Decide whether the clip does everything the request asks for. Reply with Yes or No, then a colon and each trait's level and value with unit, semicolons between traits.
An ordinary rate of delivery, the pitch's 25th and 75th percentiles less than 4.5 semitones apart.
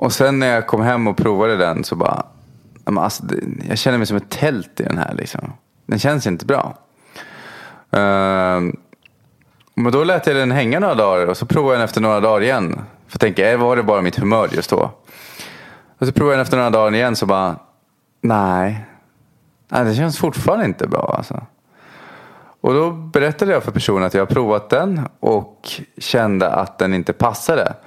No: average, 190 wpm; average, 4.9 semitones